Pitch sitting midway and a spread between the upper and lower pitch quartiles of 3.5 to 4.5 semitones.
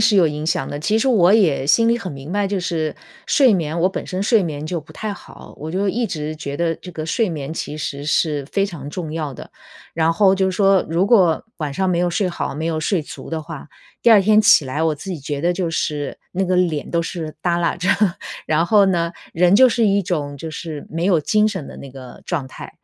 Yes: medium, 170 Hz; average, 4.0 semitones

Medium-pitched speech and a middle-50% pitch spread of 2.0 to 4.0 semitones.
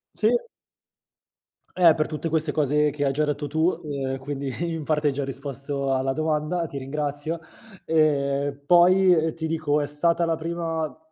Yes: medium, 150 Hz; narrow, 2.4 semitones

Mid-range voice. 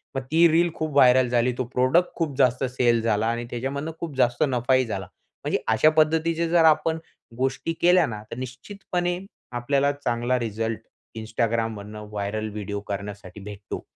No: low, 125 Hz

